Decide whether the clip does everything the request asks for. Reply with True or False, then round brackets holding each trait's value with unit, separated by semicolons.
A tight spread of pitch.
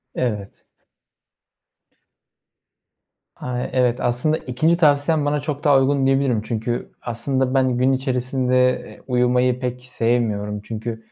True (1.9 semitones)